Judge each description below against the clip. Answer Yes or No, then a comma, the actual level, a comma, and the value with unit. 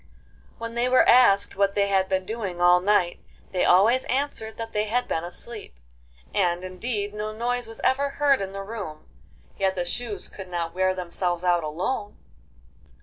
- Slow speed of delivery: No, average, 175 wpm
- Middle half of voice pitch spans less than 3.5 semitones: No, average, 4.1 semitones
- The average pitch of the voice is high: Yes, high, 200 Hz